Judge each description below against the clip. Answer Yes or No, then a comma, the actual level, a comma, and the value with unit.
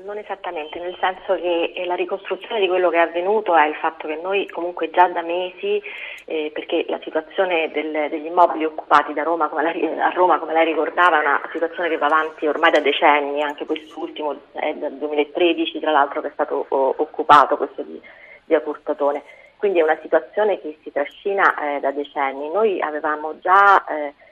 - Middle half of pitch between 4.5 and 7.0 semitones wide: No, average, 3.0 semitones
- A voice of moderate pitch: Yes, medium, 160 Hz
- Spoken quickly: Yes, fast, 185 wpm